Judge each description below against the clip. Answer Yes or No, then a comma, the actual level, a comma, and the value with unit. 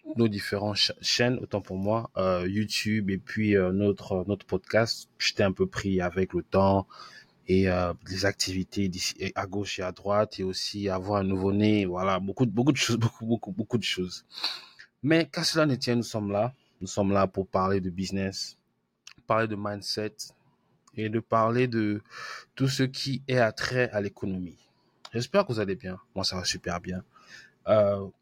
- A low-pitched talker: Yes, low, 100 Hz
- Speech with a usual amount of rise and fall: Yes, average, 3.2 semitones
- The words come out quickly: No, average, 190 wpm